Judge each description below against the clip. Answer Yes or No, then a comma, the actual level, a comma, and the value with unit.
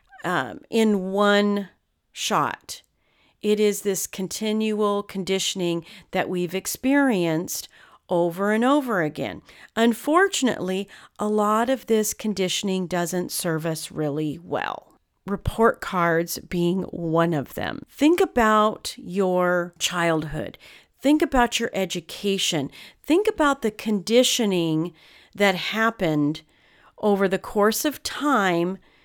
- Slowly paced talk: Yes, slow, 105 wpm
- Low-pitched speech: No, high, 195 Hz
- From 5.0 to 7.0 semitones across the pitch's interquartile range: No, average, 4.2 semitones